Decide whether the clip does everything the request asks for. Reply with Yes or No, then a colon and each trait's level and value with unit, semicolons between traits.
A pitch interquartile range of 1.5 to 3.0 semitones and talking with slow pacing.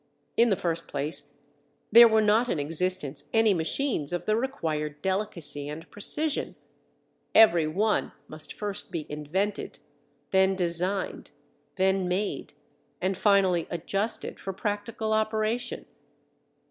No: average, 4.7 semitones; slow, 120 wpm